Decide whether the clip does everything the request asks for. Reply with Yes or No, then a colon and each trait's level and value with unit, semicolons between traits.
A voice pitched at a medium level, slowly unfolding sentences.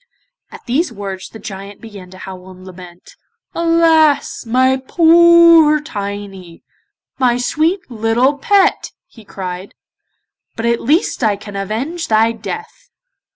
No: high, 230 Hz; slow, 125 wpm